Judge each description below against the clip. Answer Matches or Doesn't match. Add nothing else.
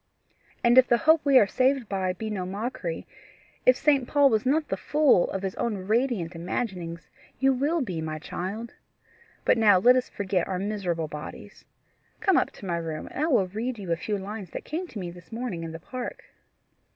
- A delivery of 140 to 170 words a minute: Doesn't match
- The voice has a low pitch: Doesn't match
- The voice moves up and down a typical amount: Doesn't match